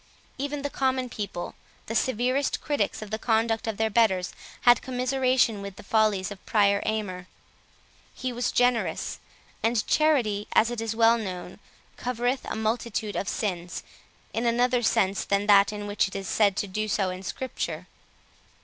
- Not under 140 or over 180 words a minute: Yes, average, 165 wpm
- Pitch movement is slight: No, average, 3.4 semitones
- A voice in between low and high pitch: No, high, 220 Hz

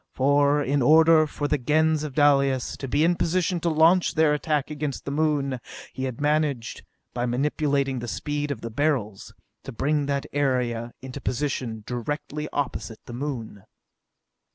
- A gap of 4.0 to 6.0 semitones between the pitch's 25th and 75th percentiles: No, average, 2.9 semitones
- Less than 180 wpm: Yes, average, 160 wpm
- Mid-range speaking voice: Yes, medium, 145 Hz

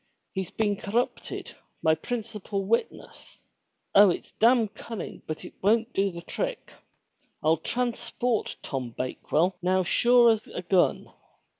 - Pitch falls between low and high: No, high, 205 Hz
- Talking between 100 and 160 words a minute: Yes, slow, 135 wpm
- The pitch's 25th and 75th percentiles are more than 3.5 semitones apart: Yes, average, 4.6 semitones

